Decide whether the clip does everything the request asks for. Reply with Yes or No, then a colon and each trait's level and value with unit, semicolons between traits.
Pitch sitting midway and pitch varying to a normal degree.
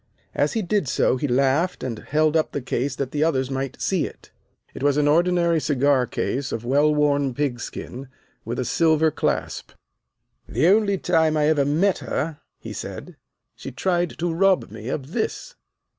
Yes: medium, 150 Hz; average, 4.0 semitones